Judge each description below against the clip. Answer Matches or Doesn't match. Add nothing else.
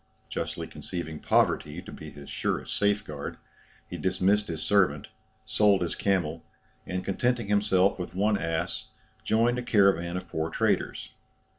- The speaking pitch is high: Doesn't match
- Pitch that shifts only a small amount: Doesn't match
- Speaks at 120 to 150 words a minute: Matches